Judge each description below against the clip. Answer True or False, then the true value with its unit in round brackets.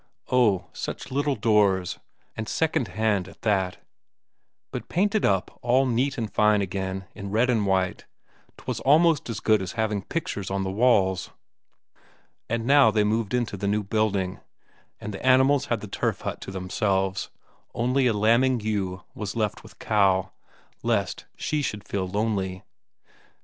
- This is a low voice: True (105 Hz)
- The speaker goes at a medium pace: True (155 wpm)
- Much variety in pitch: False (4.0 semitones)